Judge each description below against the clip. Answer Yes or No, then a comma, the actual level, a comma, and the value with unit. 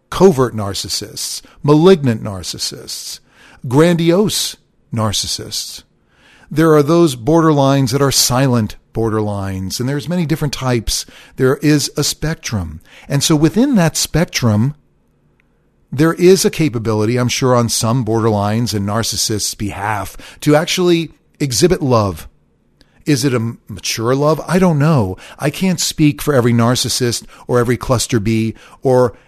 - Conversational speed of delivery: No, slow, 130 wpm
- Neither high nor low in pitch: No, low, 125 Hz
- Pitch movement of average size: No, wide, 5.8 semitones